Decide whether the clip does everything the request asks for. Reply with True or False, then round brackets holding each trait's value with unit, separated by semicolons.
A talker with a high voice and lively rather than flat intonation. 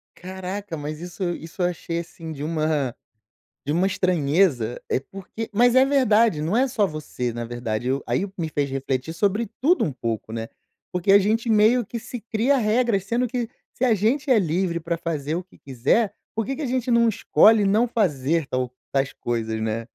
False (180 Hz; 7.5 semitones)